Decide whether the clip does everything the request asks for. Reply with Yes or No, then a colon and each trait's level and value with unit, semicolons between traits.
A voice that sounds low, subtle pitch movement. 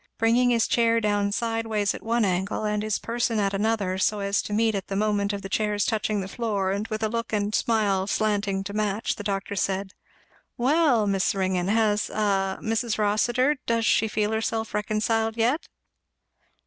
No: high, 210 Hz; narrow, 2.0 semitones